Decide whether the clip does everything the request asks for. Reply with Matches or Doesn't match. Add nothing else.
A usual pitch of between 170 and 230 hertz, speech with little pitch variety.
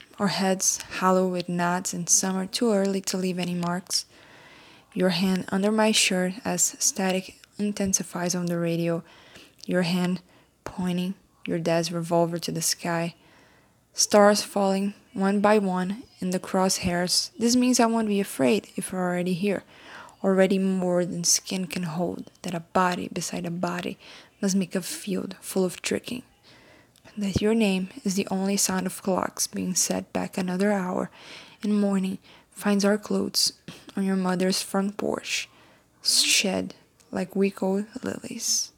Matches